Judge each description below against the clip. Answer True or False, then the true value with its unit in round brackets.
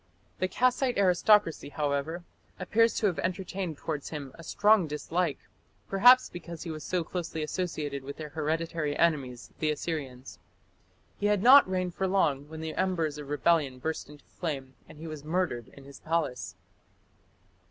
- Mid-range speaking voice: True (160 Hz)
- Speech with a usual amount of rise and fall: True (4.0 semitones)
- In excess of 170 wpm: False (160 wpm)